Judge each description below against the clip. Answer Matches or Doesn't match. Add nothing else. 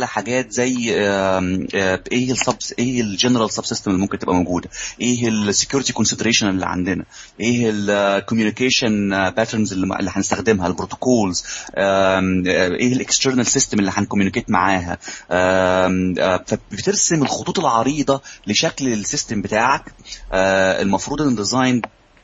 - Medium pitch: Doesn't match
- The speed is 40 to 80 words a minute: Doesn't match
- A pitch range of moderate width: Matches